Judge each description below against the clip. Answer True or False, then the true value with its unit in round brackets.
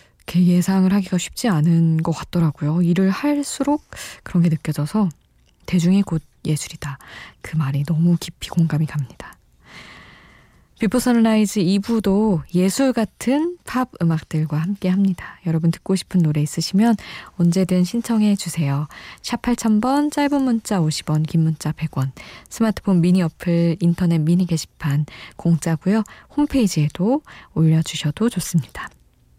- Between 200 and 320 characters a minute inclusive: True (285 characters per minute)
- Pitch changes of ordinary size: True (4.9 semitones)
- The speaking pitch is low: False (175 Hz)